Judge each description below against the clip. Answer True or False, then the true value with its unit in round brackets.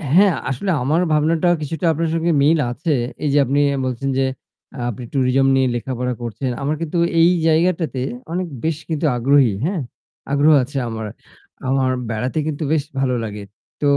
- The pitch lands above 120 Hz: True (140 Hz)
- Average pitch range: True (4.1 semitones)